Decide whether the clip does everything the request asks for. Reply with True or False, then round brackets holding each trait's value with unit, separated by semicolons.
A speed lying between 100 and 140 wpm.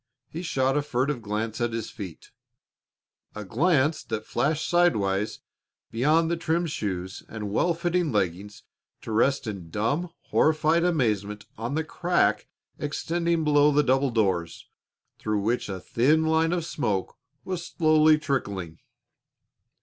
True (135 wpm)